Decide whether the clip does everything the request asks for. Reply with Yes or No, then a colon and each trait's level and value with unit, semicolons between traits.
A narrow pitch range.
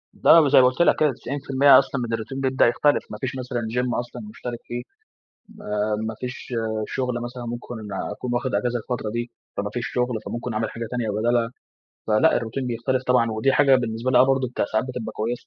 Yes: narrow, 2.2 semitones